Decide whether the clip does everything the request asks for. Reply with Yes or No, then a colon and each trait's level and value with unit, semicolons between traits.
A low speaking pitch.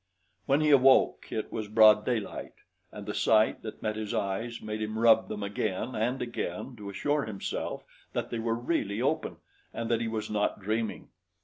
Yes: low, 110 Hz